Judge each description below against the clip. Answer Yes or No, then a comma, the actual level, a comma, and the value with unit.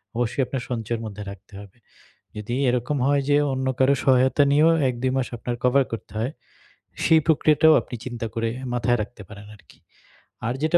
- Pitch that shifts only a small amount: No, average, 3.5 semitones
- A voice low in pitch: Yes, low, 125 Hz